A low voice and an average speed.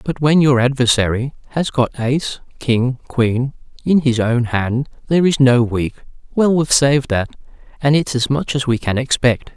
Yes: low, 130 Hz; average, 180 wpm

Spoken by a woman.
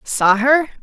Yes: female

